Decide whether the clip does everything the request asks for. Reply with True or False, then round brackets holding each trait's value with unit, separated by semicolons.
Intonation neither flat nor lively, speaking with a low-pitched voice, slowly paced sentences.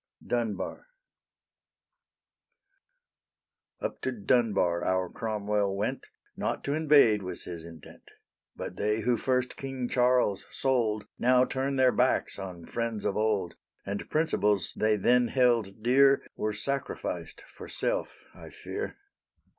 True (4.0 semitones; 115 Hz; 125 wpm)